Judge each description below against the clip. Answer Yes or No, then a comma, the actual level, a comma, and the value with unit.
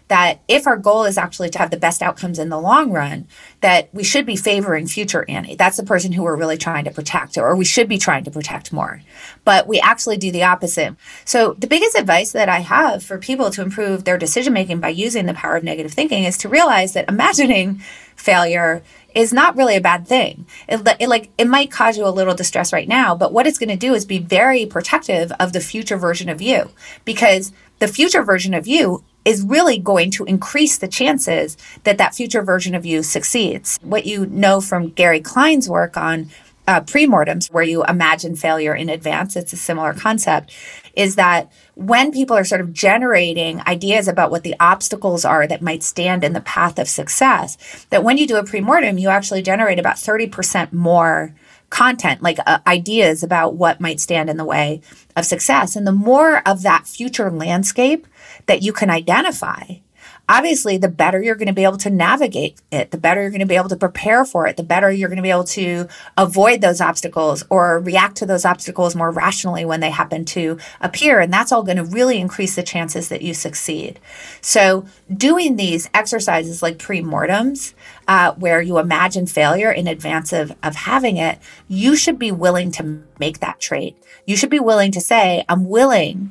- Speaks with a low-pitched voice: No, medium, 185 Hz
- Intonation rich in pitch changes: No, average, 4.4 semitones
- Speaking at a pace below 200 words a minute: No, fast, 205 wpm